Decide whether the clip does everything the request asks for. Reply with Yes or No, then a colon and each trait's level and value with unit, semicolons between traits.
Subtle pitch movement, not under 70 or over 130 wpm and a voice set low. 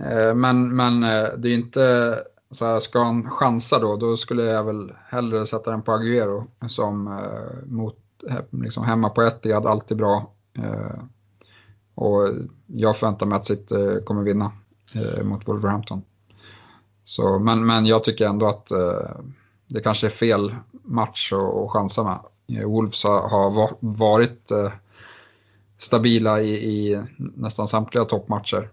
Yes: narrow, 2.0 semitones; slow, 125 wpm; low, 110 Hz